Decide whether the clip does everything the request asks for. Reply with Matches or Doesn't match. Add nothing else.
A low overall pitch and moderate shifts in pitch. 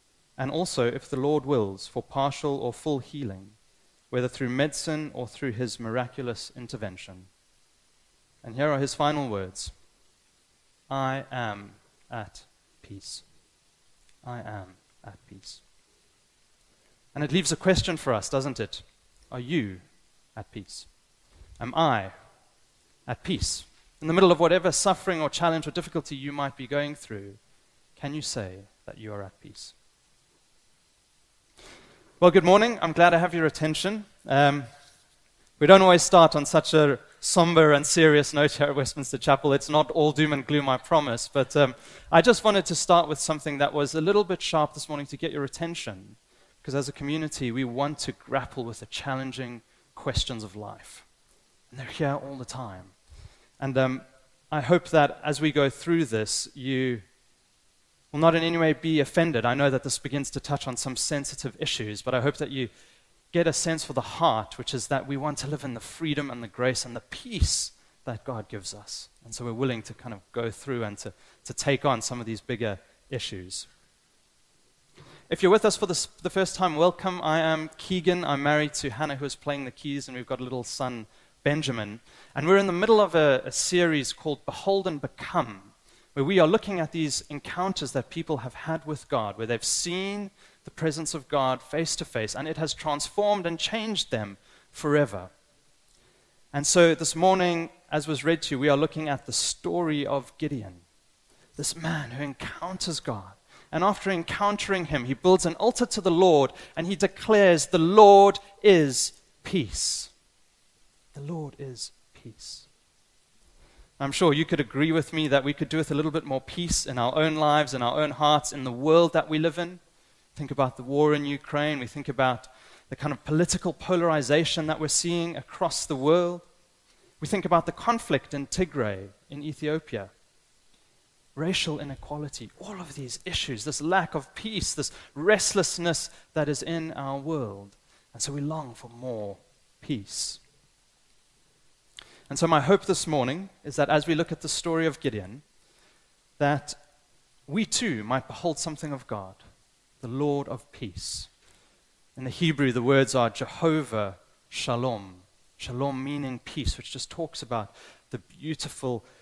Doesn't match